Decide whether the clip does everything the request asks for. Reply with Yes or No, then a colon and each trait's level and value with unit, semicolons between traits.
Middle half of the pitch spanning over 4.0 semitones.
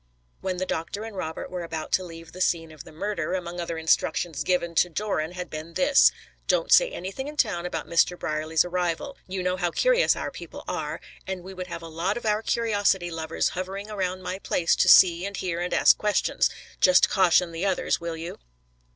No: average, 2.8 semitones